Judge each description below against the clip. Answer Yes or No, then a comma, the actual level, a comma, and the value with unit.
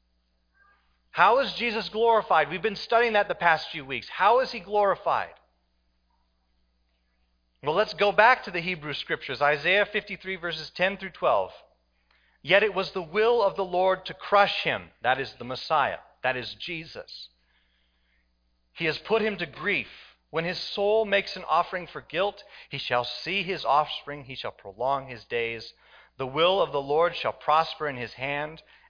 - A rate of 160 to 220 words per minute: Yes, average, 170 wpm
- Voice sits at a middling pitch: Yes, medium, 165 Hz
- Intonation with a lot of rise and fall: Yes, wide, 8.9 semitones